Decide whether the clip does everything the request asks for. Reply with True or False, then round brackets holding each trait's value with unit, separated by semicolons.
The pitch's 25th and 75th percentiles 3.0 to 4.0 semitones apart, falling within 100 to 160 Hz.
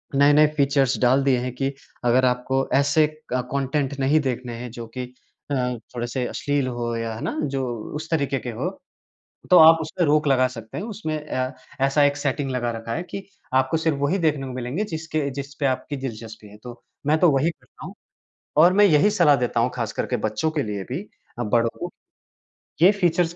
True (3.7 semitones; 135 Hz)